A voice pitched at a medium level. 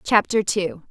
No: high, 200 Hz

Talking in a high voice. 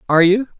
Yes: high, 195 Hz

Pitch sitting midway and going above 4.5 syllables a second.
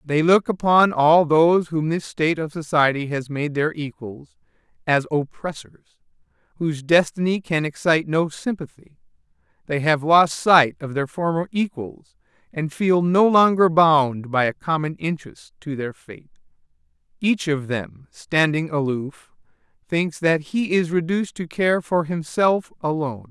No: medium, 160 Hz; 4.4 syllables/s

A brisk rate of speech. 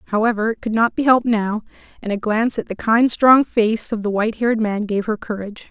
Yes: fast, 240 wpm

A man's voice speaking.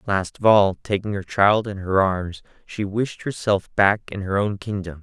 Yes: male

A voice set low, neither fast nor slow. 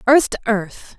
No: high, 230 Hz; average, 185 wpm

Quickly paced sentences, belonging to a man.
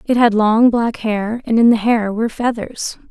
No: fast, 215 wpm; female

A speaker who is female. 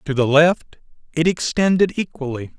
No: male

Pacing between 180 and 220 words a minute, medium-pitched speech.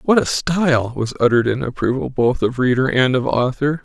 No: fast, 205 wpm; low, 130 Hz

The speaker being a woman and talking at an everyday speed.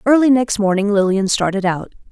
Yes: female; average, 170 wpm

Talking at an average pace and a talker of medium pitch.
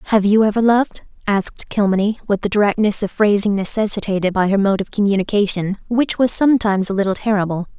No: average, 175 wpm; high, 205 Hz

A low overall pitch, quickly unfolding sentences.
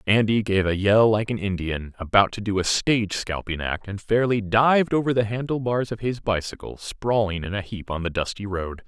Yes: low, 105 Hz; fast, 210 wpm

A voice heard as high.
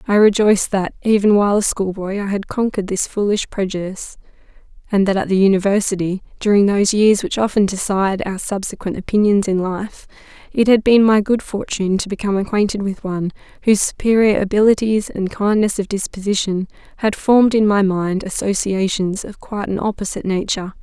Yes: high, 200 Hz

